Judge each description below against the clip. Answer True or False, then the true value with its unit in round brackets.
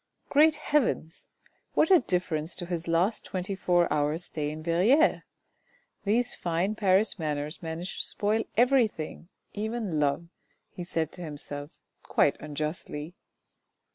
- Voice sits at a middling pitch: True (175 Hz)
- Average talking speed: False (130 wpm)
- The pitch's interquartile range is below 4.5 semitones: False (5.4 semitones)